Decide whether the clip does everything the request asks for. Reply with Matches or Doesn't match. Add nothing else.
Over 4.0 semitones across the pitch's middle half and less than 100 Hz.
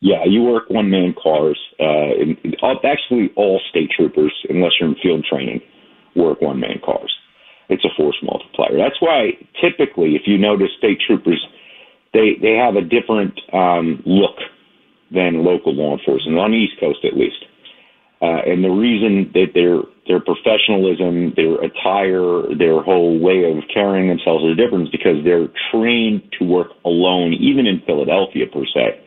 Doesn't match